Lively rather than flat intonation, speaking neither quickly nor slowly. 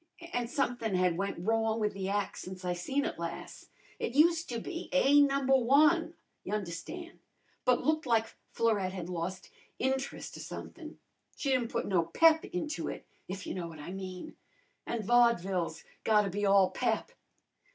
Yes: wide, 6.2 semitones; average, 165 wpm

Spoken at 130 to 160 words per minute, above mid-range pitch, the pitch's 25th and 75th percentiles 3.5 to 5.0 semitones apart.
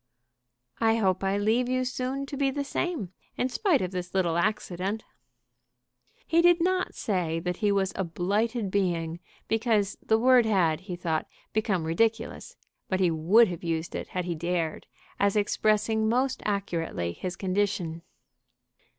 Yes: average, 155 wpm; high, 200 Hz; average, 4.6 semitones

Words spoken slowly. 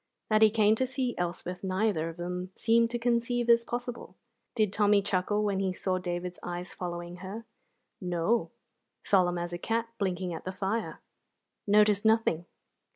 No: average, 160 wpm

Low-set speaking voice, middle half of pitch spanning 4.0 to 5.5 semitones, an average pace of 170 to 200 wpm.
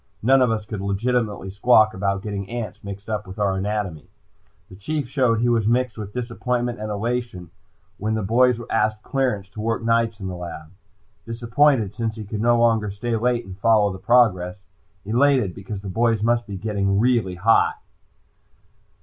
No: low, 110 Hz; average, 3.2 semitones; average, 175 wpm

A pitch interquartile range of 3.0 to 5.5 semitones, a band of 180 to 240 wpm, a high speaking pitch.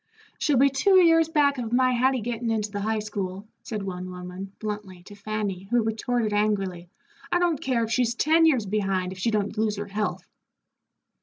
Yes: average, 4.0 semitones; average, 190 wpm; high, 215 Hz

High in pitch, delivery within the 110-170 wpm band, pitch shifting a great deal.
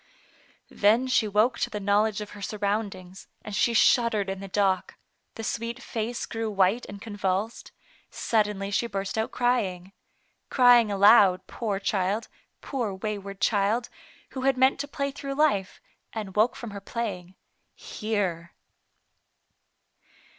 No: high, 210 Hz; average, 145 wpm; average, 3.0 semitones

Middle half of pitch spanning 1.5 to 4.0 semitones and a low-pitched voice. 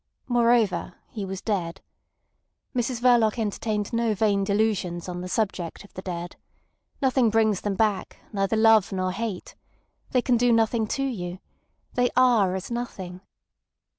No: average, 3.7 semitones; high, 215 Hz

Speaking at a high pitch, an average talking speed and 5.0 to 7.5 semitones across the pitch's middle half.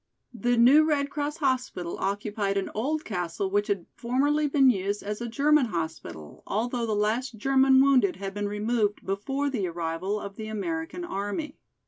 Yes: high, 220 Hz; average, 165 wpm; average, 5.3 semitones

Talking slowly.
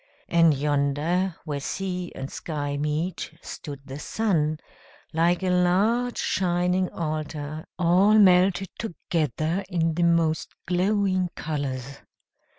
Yes: slow, 110 wpm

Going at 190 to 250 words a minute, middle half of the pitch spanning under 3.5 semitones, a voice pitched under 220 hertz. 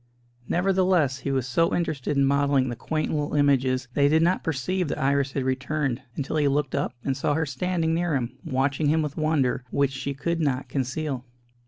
Yes: average, 200 wpm; average, 2.9 semitones; medium, 140 Hz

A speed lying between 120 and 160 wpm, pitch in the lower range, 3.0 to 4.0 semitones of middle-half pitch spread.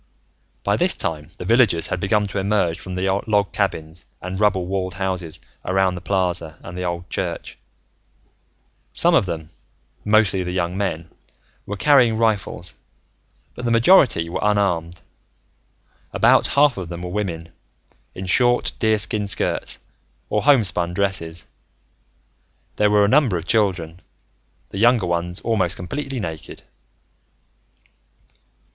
Yes: slow, 135 wpm; very low, 95 Hz; average, 3.5 semitones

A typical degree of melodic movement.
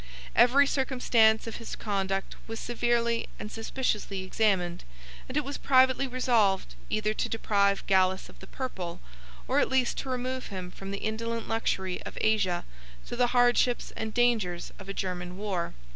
Yes: average, 4.1 semitones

